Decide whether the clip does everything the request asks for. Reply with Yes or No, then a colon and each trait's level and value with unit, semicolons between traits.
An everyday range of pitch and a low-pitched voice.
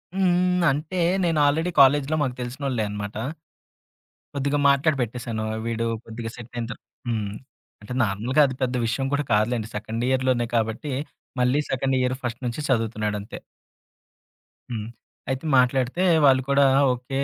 Yes: average, 3.5 semitones; low, 125 Hz